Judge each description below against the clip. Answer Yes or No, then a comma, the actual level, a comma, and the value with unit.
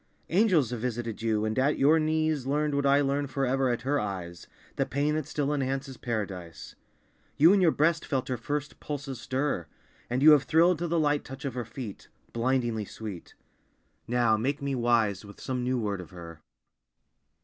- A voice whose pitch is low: Yes, low, 130 Hz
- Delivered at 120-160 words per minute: No, average, 185 wpm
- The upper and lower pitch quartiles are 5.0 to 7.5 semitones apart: No, average, 4.3 semitones